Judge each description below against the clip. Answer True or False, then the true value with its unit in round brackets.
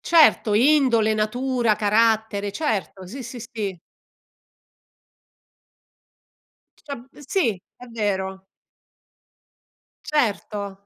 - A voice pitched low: False (220 Hz)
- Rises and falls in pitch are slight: False (3.7 semitones)